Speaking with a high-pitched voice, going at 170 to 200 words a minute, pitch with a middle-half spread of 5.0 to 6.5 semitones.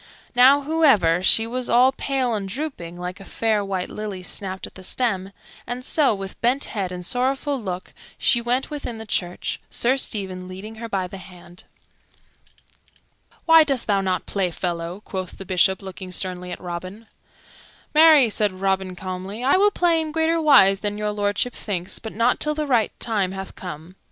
Yes: high, 205 Hz; average, 180 wpm; average, 5.3 semitones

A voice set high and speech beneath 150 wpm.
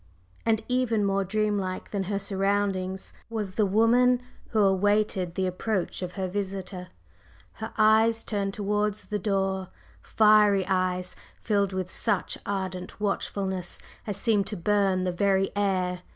Yes: high, 200 Hz; average, 140 wpm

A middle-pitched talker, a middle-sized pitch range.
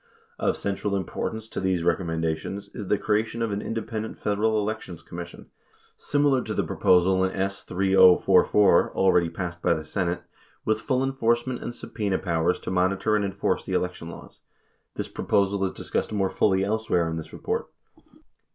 No: low, 100 Hz; average, 3.3 semitones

